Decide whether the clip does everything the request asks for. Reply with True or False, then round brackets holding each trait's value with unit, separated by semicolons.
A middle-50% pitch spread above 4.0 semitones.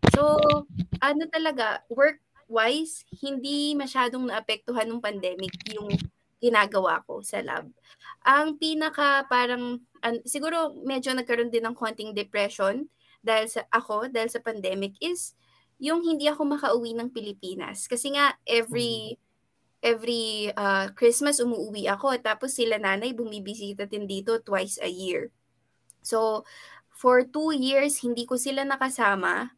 True (4.4 semitones)